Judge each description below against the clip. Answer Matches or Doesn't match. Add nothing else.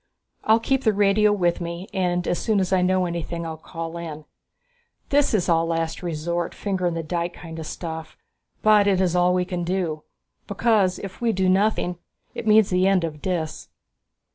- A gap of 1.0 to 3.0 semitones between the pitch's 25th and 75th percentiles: Matches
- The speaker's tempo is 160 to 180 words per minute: Doesn't match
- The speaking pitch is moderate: Matches